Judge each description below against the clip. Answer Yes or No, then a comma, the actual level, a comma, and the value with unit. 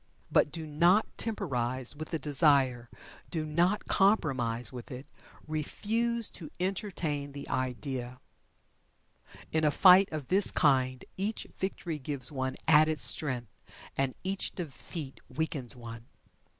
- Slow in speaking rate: Yes, slow, 125 wpm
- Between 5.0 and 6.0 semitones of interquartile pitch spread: Yes, wide, 5.4 semitones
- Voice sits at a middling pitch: Yes, medium, 150 Hz